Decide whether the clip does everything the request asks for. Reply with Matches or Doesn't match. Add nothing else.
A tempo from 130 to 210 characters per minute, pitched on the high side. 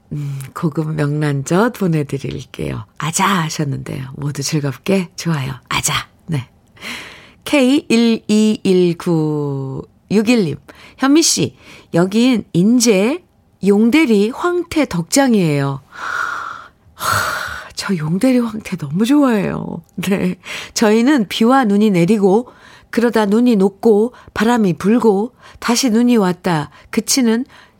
Matches